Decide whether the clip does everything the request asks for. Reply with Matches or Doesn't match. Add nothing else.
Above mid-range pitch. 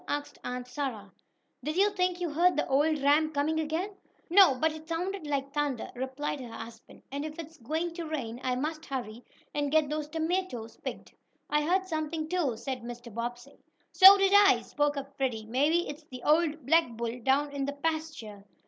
Matches